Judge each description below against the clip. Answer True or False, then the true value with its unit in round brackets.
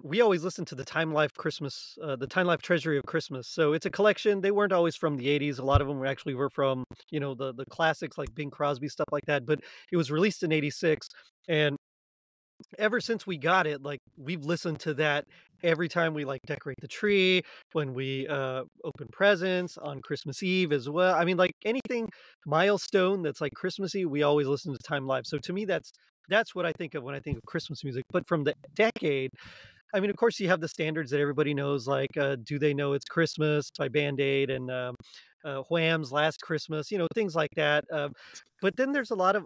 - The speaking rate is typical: False (230 wpm)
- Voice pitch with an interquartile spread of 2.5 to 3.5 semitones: False (4.2 semitones)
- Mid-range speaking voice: True (155 Hz)